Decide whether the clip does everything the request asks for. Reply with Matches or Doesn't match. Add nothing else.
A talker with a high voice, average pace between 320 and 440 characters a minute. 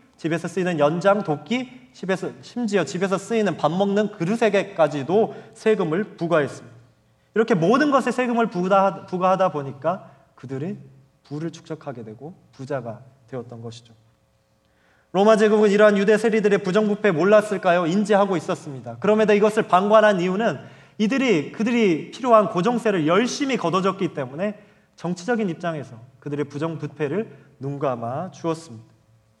Doesn't match